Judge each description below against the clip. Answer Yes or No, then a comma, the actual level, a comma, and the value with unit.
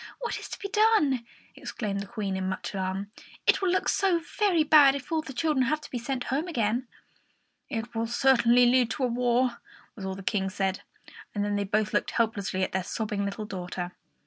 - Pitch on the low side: No, high, 235 Hz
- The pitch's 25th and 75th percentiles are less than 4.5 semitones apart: No, wide, 5.4 semitones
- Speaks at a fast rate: Yes, fast, 210 wpm